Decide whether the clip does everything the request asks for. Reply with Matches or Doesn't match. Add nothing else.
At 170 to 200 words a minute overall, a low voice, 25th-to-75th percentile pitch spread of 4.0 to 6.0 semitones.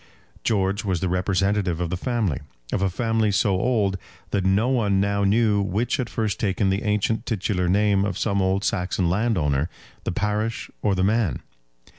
Doesn't match